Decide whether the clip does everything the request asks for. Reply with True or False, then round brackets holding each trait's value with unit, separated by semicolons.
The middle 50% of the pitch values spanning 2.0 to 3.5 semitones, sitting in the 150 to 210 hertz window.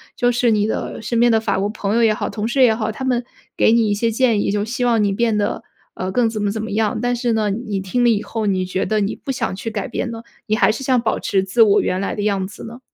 False (2.5 semitones; 220 Hz)